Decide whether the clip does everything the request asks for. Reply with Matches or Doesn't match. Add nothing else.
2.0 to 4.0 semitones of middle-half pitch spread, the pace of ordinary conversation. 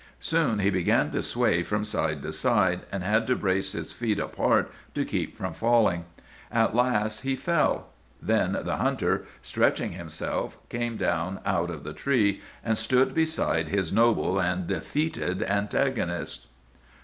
Doesn't match